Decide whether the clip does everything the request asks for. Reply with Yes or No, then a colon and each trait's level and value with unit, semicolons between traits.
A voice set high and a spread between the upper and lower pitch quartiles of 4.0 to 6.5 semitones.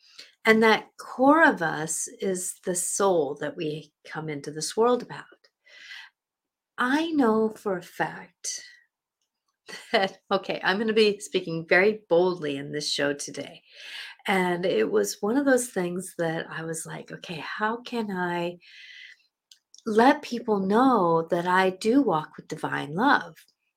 Yes: high, 195 Hz; wide, 5.6 semitones